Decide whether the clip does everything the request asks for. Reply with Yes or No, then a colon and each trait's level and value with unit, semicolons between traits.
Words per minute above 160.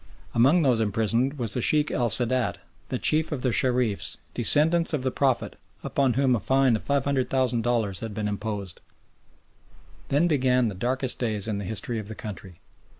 Yes: average, 180 wpm